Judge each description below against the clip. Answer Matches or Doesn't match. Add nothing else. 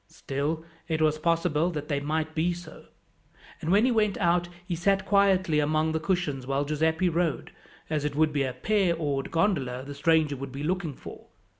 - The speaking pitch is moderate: Matches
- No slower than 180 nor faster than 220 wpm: Matches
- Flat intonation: Doesn't match